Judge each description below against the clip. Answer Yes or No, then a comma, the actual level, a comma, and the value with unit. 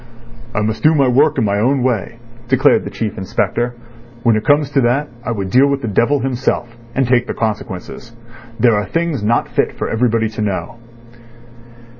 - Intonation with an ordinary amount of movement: Yes, average, 3.7 semitones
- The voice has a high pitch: No, low, 120 Hz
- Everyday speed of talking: Yes, average, 190 wpm